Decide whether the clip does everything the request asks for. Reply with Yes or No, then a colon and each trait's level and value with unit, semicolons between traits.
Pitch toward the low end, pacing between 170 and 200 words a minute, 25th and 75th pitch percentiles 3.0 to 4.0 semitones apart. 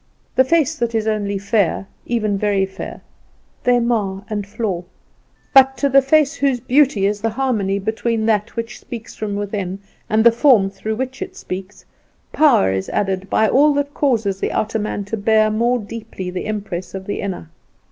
No: high, 215 Hz; average, 180 wpm; average, 3.5 semitones